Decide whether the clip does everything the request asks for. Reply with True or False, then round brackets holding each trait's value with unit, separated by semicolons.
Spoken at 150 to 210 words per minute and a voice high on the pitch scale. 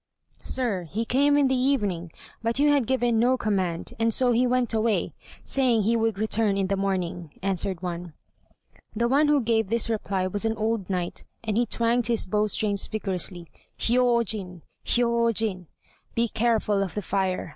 True (170 wpm; 220 Hz)